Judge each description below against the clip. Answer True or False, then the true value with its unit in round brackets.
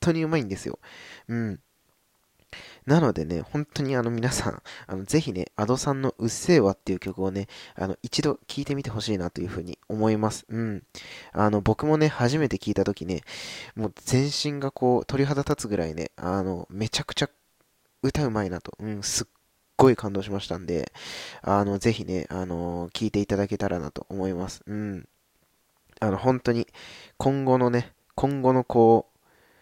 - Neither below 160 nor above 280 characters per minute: False (340 characters per minute)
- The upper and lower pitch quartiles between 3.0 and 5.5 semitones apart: True (5.2 semitones)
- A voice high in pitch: False (110 Hz)